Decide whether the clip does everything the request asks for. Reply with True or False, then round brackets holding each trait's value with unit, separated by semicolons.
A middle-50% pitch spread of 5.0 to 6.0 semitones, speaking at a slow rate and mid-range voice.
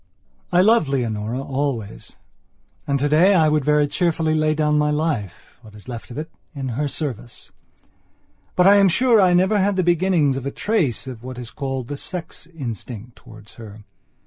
False (5.6 semitones; 180 wpm; 145 Hz)